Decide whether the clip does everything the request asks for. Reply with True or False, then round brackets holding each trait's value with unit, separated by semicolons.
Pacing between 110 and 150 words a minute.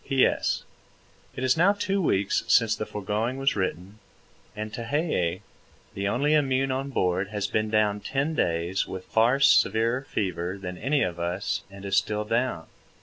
False (160 wpm)